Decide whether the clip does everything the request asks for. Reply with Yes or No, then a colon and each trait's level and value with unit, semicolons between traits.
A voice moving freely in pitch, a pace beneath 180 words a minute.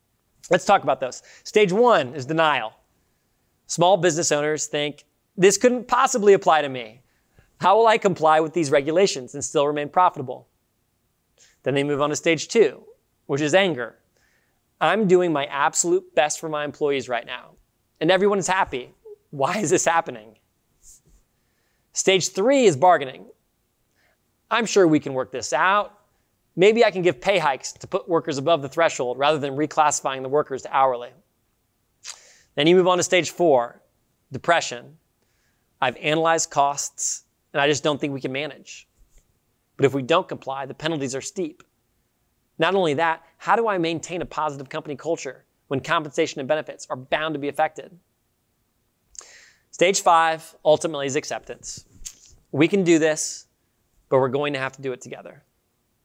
No: average, 4.3 semitones; average, 165 wpm